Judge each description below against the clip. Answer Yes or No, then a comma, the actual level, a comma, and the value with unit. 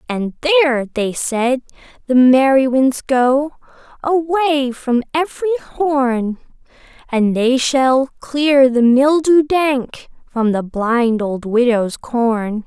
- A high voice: Yes, very high, 260 Hz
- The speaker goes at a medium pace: No, slow, 120 wpm